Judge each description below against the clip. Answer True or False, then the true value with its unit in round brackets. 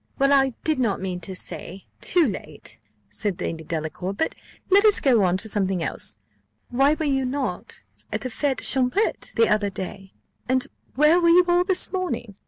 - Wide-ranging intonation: True (7.8 semitones)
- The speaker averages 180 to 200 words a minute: True (185 wpm)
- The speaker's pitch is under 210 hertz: False (250 Hz)